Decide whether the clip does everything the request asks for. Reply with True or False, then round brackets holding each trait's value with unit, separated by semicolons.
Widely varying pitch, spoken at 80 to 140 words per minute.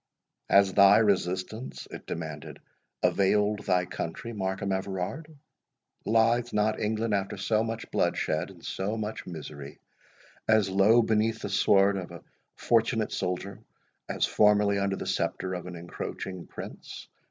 False (2.8 semitones; 135 wpm)